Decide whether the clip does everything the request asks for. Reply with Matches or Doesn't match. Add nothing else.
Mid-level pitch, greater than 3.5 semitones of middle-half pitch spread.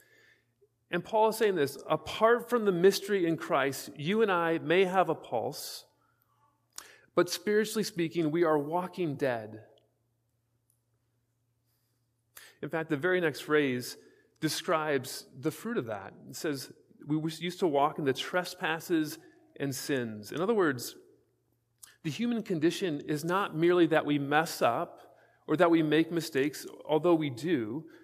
Matches